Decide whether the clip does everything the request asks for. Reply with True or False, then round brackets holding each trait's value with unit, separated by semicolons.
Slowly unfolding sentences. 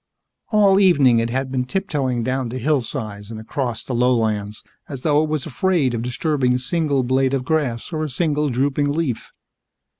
False (180 wpm)